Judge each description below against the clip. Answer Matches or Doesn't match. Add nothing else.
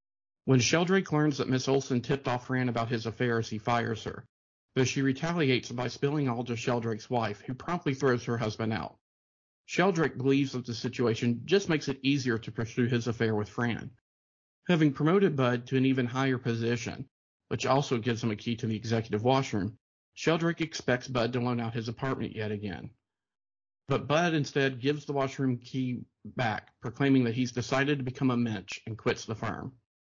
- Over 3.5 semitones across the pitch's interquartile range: Doesn't match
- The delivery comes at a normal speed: Matches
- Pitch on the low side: Matches